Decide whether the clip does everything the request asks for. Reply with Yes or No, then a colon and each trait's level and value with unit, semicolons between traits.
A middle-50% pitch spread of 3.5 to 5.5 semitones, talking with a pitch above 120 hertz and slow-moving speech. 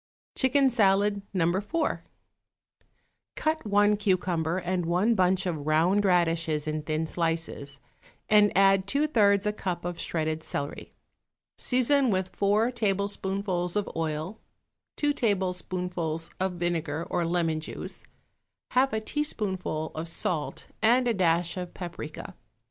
Yes: average, 4.0 semitones; medium, 185 Hz; slow, 125 wpm